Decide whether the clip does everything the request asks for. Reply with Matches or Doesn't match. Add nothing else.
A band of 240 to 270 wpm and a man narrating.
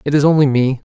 Matches